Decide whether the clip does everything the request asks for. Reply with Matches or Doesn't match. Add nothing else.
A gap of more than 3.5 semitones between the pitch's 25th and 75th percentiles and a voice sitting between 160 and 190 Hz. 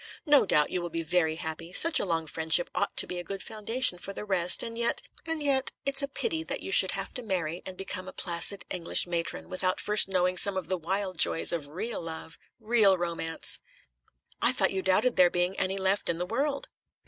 Matches